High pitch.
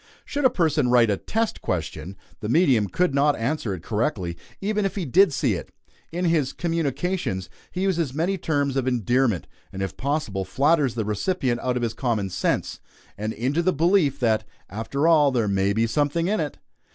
No: low, 135 Hz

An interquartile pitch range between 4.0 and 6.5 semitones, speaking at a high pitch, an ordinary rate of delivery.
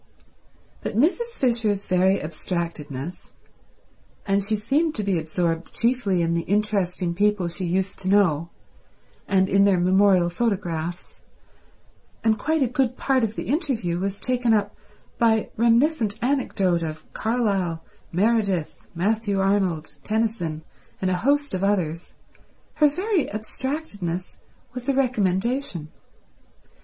No: average, 4.9 semitones; high, 200 Hz; slow, 120 wpm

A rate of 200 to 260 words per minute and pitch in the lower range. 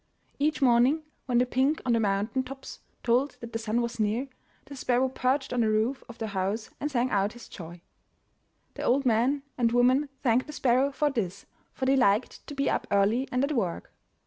No: fast, 205 wpm; high, 245 Hz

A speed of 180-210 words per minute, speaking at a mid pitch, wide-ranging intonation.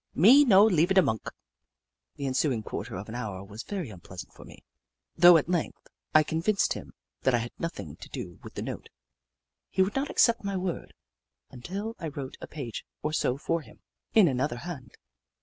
Yes: average, 195 wpm; medium, 155 Hz; wide, 7.7 semitones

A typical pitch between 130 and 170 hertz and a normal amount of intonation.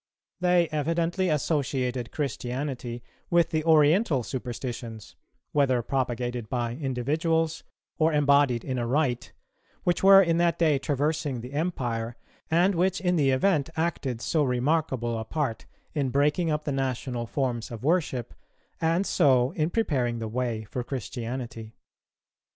Yes: low, 135 Hz; average, 4.8 semitones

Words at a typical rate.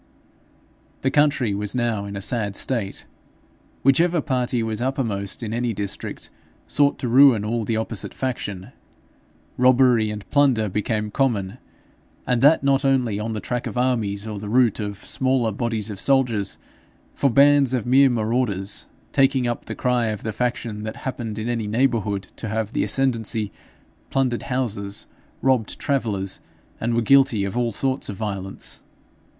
Yes: average, 160 wpm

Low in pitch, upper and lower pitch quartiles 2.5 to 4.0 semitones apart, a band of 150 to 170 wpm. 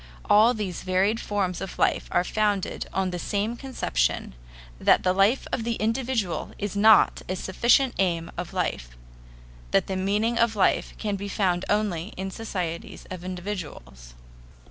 No: high, 195 Hz; average, 3.2 semitones; average, 155 wpm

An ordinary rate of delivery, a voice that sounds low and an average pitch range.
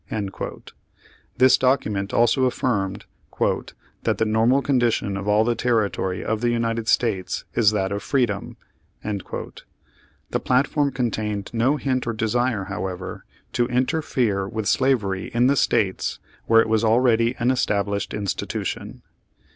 No: slow, 130 wpm; low, 115 Hz; average, 3.5 semitones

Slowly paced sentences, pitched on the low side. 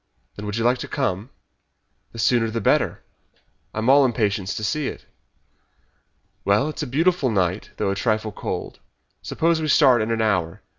No: average, 185 wpm; low, 115 Hz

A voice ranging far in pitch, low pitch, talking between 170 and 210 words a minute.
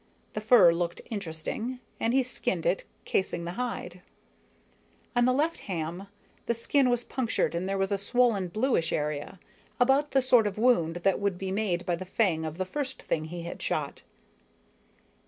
No: wide, 6.1 semitones; high, 200 Hz; average, 180 wpm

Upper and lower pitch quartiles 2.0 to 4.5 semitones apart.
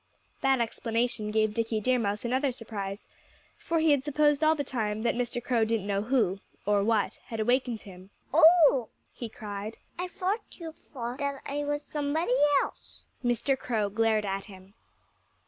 No: average, 4.9 semitones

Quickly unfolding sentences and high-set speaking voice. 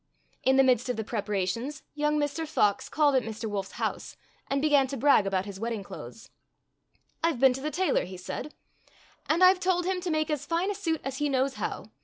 Yes: fast, 230 wpm; very high, 275 Hz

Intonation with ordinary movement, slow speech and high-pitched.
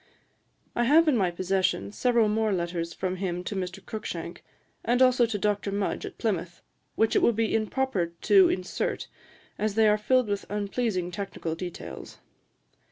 No: average, 3.9 semitones; average, 165 wpm; high, 205 Hz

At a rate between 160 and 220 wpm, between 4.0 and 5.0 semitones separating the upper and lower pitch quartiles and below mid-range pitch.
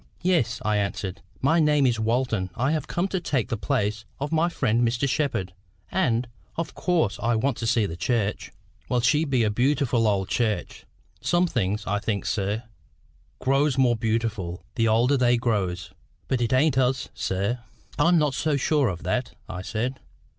Yes: average, 180 wpm; average, 4.6 semitones; low, 120 Hz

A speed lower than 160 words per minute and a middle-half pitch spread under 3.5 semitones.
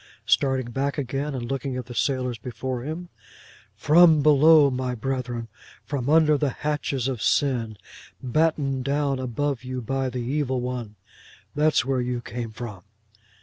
Yes: average, 150 wpm; average, 2.8 semitones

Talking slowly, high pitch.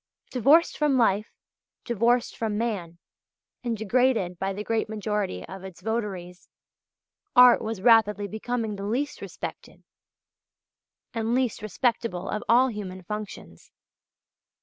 Yes: slow, 120 wpm; high, 220 Hz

